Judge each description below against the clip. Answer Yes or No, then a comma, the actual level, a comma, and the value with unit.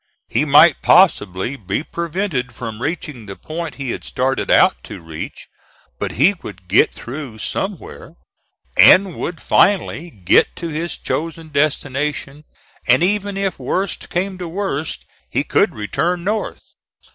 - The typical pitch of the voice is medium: Yes, medium, 155 Hz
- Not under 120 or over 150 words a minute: Yes, average, 140 wpm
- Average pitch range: No, wide, 6.3 semitones